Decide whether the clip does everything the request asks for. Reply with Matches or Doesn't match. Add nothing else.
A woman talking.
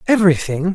Doesn't match